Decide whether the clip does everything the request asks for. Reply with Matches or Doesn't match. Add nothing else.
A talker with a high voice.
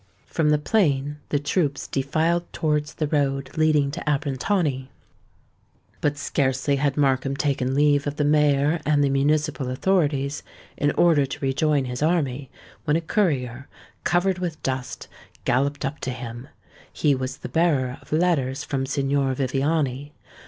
Doesn't match